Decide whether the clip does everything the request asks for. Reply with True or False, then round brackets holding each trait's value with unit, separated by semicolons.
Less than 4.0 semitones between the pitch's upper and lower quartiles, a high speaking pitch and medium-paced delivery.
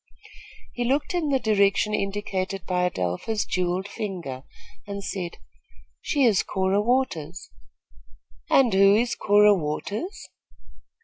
False (3.5 semitones; 200 Hz; 115 wpm)